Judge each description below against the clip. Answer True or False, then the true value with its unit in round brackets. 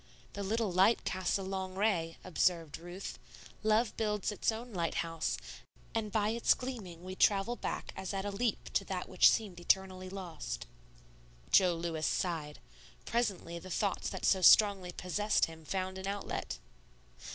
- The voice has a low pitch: False (190 Hz)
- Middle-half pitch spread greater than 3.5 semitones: False (3.1 semitones)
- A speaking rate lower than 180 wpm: True (155 wpm)